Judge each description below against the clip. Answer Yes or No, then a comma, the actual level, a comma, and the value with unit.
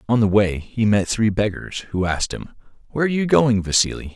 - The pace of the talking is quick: Yes, fast, 215 wpm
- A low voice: Yes, low, 110 Hz